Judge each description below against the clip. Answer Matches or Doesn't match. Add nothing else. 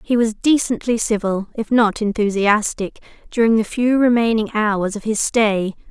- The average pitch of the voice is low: Doesn't match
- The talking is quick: Doesn't match